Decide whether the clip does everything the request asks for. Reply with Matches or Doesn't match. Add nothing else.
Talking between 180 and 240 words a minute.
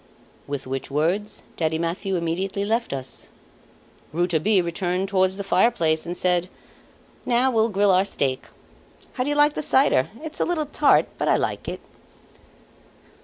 Doesn't match